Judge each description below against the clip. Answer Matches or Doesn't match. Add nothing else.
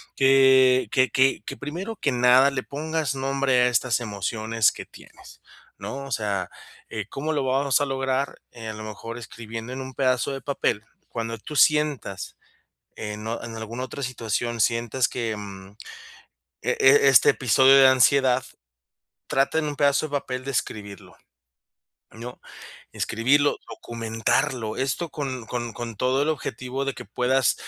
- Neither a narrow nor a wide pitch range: Matches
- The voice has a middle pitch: Doesn't match